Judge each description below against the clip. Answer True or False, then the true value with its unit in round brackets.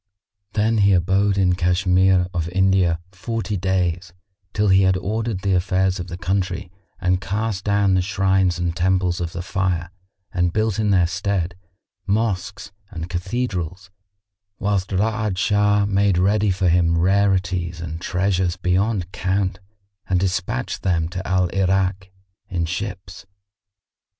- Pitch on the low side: True (95 Hz)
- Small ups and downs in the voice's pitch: True (2.0 semitones)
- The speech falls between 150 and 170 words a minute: False (140 wpm)